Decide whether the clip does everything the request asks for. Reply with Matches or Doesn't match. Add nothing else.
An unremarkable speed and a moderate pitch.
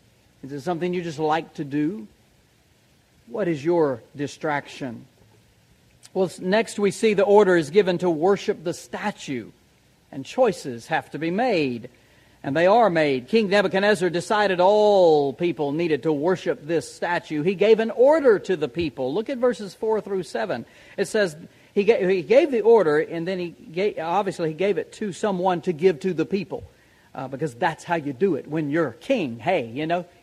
Matches